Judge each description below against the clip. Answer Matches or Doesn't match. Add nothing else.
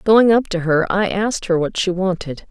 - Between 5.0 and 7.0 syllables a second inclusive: Matches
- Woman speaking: Matches